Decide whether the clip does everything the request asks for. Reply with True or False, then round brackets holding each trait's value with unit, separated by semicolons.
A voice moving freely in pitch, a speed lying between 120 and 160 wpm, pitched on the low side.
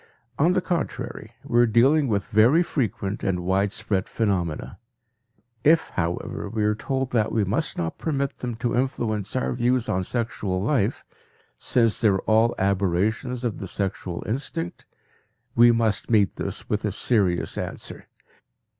False (4.1 semitones; 150 wpm; 110 Hz)